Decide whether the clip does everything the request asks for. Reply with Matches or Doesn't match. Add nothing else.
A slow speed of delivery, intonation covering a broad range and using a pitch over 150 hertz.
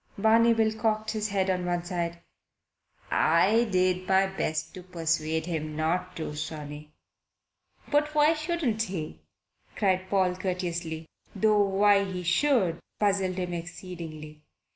Doesn't match